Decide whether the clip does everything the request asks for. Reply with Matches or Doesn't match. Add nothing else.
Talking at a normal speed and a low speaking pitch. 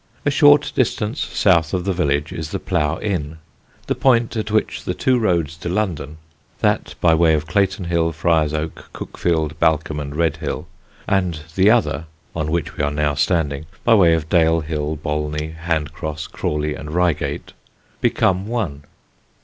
Matches